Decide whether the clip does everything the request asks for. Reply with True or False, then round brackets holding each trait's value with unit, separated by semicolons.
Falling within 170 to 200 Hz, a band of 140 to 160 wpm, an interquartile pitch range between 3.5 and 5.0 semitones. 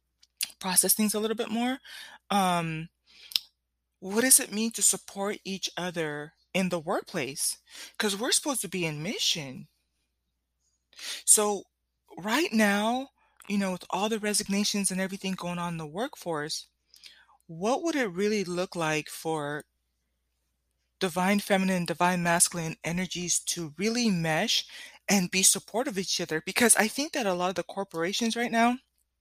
True (185 Hz; 150 wpm; 4.7 semitones)